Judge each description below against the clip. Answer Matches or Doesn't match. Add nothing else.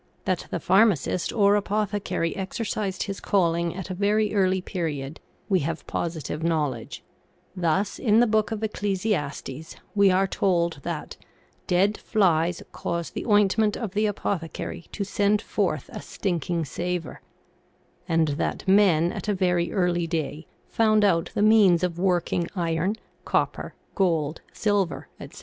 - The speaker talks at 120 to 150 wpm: Matches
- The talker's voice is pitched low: Doesn't match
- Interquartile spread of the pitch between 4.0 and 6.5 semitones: Doesn't match